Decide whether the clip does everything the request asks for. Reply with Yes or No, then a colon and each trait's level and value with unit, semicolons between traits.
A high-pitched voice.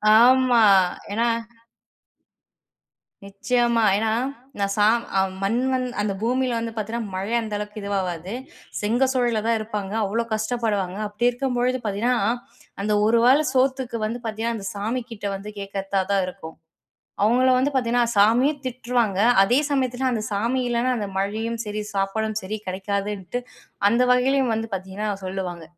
Yes: high, 225 Hz